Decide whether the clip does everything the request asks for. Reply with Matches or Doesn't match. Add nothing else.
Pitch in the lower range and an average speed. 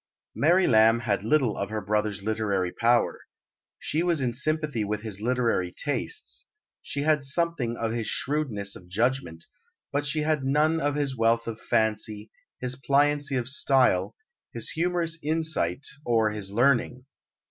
Matches